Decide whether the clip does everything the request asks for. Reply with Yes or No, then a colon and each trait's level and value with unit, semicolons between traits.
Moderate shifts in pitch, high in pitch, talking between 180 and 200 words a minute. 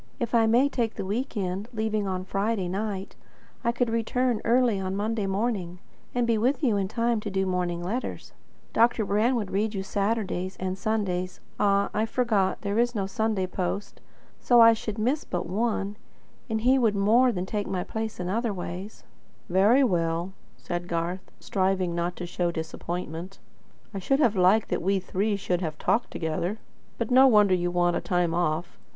Yes: average, 3.8 semitones; high, 200 Hz; average, 185 wpm